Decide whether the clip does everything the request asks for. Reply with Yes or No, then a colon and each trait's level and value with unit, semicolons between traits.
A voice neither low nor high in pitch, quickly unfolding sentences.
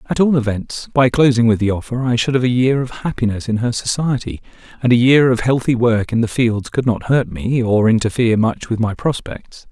No: low, 120 Hz; fast, 230 wpm